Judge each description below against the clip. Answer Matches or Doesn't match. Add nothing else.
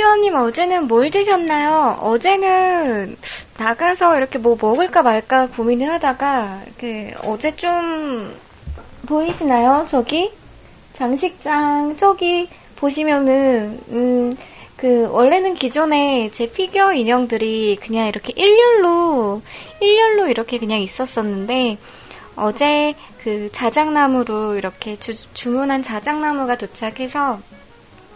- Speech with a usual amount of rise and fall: Doesn't match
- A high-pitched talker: Matches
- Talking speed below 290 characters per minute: Matches